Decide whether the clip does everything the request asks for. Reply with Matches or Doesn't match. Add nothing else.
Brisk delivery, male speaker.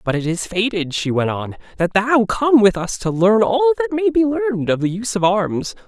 Matches